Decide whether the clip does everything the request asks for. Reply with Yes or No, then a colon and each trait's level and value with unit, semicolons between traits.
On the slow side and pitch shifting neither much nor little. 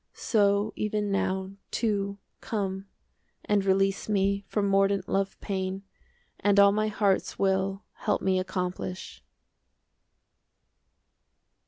No: slow, 110 wpm; narrow, 1.0 semitones